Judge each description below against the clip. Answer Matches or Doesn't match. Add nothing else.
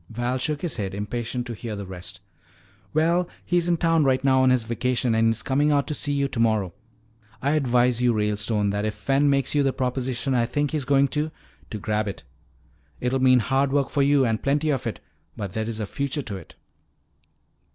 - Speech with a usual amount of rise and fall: Matches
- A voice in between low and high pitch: Doesn't match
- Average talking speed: Doesn't match